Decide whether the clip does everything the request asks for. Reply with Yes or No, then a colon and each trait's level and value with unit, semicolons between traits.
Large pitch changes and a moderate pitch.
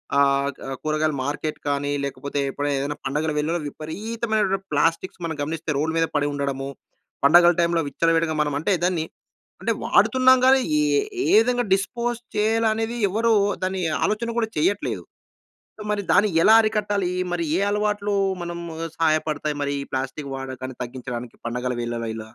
Yes: wide, 6.7 semitones; medium, 165 Hz